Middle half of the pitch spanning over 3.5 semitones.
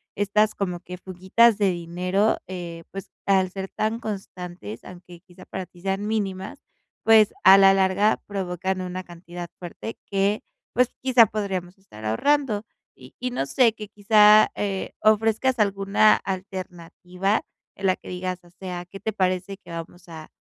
No: average, 2.8 semitones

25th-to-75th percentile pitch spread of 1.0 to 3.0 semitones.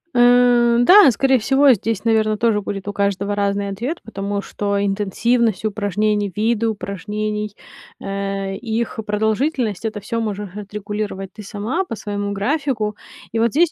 Yes: narrow, 2.6 semitones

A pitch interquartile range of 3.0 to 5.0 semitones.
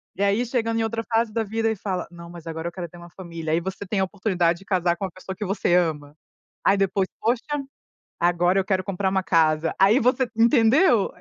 Yes: average, 4.3 semitones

